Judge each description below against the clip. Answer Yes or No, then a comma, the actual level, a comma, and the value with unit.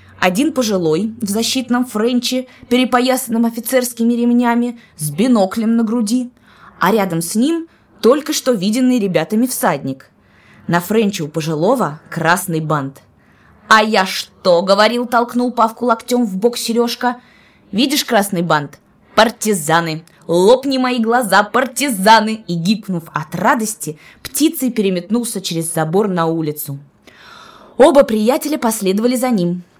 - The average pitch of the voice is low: No, high, 220 Hz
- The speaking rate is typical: Yes, average, 120 wpm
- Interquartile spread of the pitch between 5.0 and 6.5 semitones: Yes, wide, 5.6 semitones